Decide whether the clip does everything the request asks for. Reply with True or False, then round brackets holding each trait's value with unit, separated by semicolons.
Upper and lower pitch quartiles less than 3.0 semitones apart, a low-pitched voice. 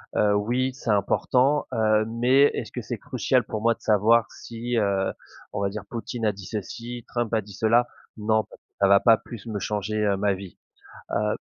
True (2.4 semitones; 110 Hz)